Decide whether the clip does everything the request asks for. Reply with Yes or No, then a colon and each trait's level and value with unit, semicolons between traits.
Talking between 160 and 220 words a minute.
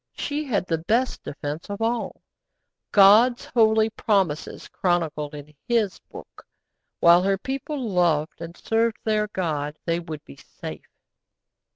No: slow, 135 wpm